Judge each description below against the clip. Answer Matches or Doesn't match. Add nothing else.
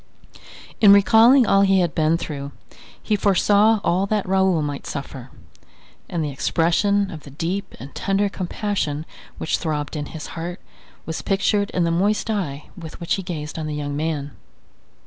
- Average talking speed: Matches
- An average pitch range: Matches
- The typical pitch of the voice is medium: Matches